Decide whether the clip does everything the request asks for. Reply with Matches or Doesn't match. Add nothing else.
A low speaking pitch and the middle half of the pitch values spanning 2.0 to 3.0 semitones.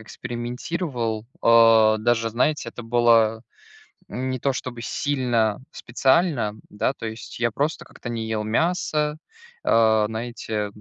Matches